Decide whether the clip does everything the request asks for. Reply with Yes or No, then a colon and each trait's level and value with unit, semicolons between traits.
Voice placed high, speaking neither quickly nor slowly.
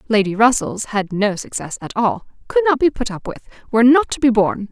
No: high, 235 Hz; fast, 230 wpm